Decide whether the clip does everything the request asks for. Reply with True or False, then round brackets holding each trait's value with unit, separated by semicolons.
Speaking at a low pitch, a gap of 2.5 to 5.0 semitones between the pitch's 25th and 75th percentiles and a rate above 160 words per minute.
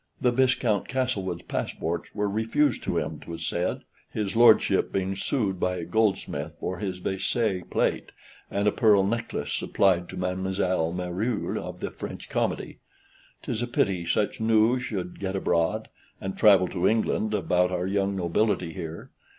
False (95 Hz; 3.3 semitones; 150 wpm)